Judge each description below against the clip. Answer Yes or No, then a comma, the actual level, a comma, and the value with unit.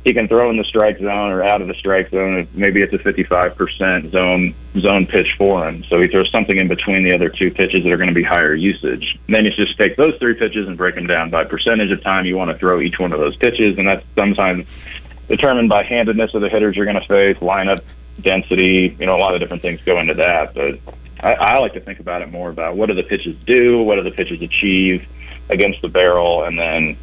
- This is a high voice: No, very low, 95 Hz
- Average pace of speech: No, fast, 255 wpm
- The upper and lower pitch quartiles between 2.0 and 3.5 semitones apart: Yes, average, 2.9 semitones